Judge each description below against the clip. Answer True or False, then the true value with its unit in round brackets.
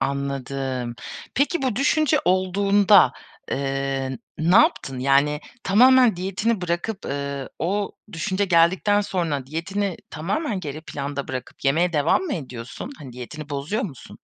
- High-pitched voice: False (165 Hz)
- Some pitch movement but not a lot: False (6.5 semitones)